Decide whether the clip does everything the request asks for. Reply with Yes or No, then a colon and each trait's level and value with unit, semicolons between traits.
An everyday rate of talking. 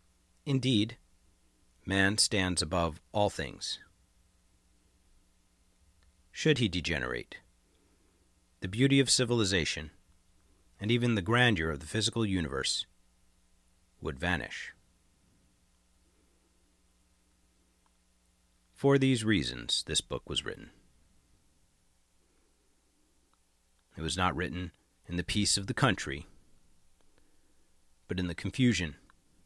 No: slow, 90 wpm